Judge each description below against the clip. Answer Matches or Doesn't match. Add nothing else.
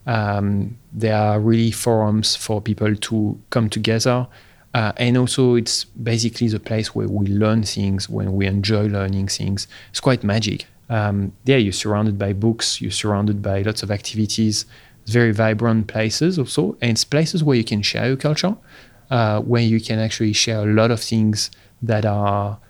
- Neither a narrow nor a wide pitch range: Doesn't match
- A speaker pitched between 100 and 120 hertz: Matches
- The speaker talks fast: Doesn't match